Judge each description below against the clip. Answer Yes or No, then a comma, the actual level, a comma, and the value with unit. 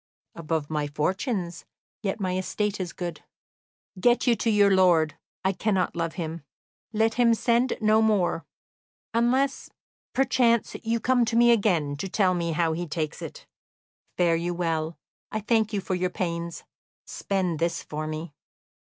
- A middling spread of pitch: Yes, average, 5.0 semitones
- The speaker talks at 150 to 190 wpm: Yes, average, 155 wpm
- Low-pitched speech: No, medium, 185 Hz